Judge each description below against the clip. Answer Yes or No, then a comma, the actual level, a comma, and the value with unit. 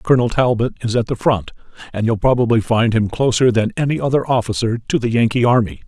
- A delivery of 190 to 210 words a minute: Yes, fast, 205 wpm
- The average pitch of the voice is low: Yes, low, 115 Hz